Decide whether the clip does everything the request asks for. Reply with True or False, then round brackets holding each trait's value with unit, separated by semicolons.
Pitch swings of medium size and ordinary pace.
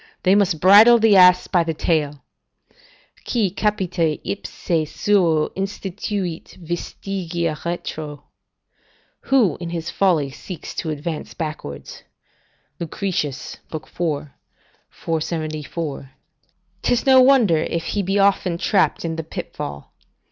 False (4.0 semitones; 110 wpm)